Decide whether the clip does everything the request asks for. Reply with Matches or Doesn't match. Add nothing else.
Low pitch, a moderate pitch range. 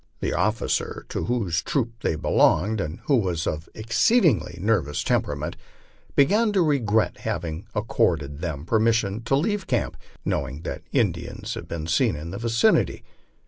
Doesn't match